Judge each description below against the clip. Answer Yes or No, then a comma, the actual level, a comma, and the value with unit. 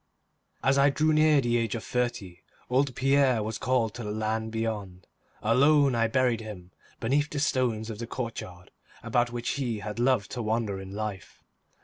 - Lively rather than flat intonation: No, average, 3.2 semitones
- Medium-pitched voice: No, low, 115 Hz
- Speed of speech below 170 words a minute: No, average, 175 wpm